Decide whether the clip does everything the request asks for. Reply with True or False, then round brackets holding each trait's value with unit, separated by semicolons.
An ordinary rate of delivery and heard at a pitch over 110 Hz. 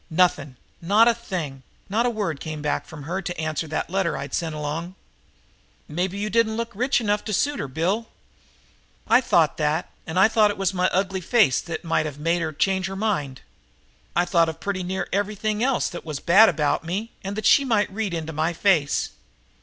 False (210 wpm; 185 Hz)